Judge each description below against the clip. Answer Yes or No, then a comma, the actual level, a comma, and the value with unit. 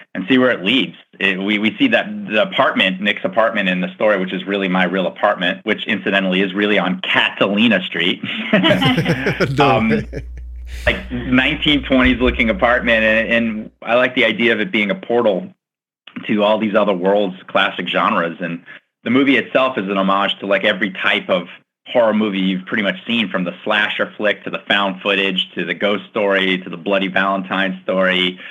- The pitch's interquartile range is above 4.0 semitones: Yes, average, 4.5 semitones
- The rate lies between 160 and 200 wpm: Yes, average, 185 wpm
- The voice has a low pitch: Yes, low, 100 Hz